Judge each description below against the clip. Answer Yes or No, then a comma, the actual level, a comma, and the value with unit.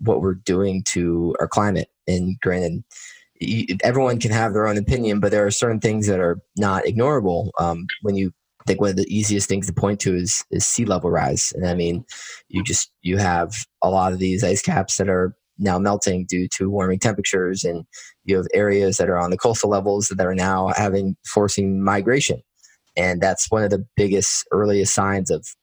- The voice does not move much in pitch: Yes, narrow, 1.9 semitones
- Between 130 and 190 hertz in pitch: No, very low, 95 Hz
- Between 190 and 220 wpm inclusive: Yes, average, 200 wpm